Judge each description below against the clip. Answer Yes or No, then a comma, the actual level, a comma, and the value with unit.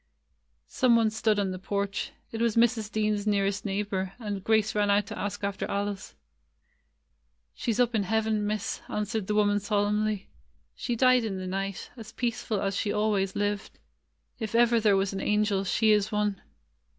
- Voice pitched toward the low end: No, high, 210 Hz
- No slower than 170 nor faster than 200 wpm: Yes, average, 175 wpm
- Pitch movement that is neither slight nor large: No, narrow, 1.7 semitones